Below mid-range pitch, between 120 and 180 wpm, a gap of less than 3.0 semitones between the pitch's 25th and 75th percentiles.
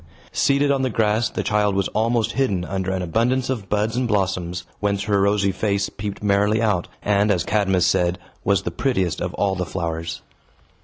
No: low, 100 Hz; average, 190 wpm; narrow, 2.6 semitones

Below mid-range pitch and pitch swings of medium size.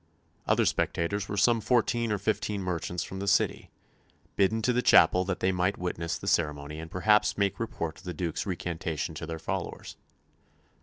Yes: very low, 95 Hz; average, 3.5 semitones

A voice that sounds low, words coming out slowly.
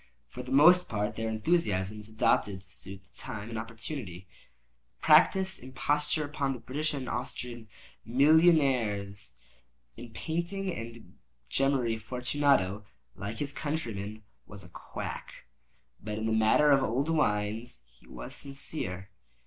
Yes: low, 115 Hz; slow, 130 wpm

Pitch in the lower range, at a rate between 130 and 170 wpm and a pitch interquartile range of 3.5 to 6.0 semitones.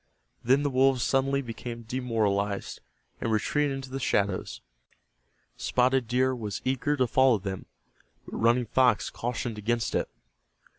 No: low, 125 Hz; slow, 135 wpm; average, 2.9 semitones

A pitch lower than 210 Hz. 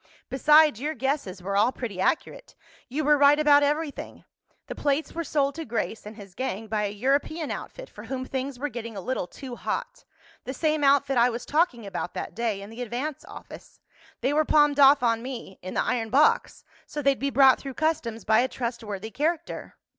No: very high, 265 Hz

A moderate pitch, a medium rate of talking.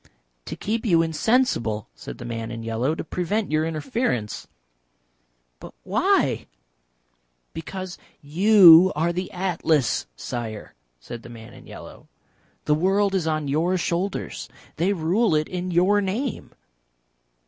No: medium, 170 Hz; slow, 130 wpm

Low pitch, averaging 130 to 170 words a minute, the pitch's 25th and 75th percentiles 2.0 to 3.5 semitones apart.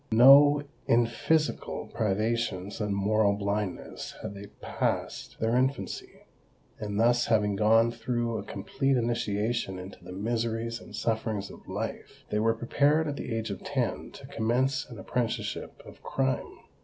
Yes: low, 115 Hz; average, 140 wpm; average, 2.9 semitones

